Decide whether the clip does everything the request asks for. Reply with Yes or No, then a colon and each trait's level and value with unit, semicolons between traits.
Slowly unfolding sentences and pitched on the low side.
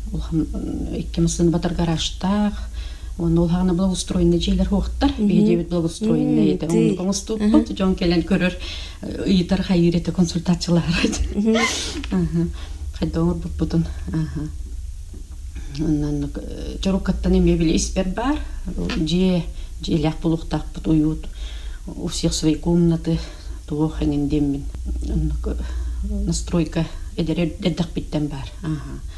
No: slow, 100 wpm; medium, 165 Hz